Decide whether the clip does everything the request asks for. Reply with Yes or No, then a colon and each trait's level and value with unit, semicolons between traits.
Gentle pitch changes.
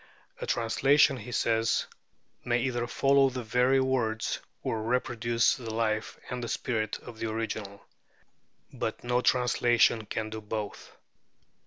Yes: narrow, 2.1 semitones